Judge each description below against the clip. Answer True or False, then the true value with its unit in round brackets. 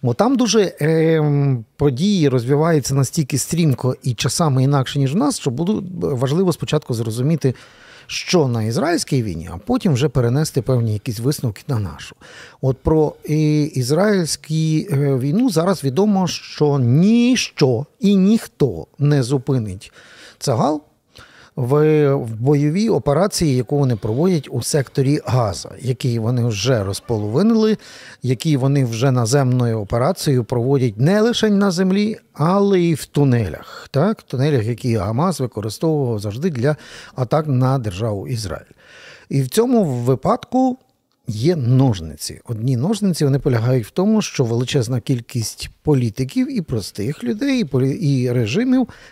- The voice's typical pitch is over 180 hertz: False (140 Hz)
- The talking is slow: False (130 wpm)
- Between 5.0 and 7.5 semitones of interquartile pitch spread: True (5.3 semitones)